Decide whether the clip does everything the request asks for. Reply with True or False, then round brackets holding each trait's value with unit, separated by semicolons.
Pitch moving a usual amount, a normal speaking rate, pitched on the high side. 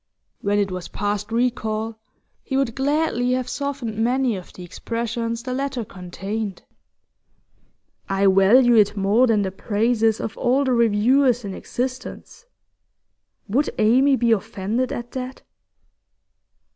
False (3.6 semitones; 130 wpm; 230 Hz)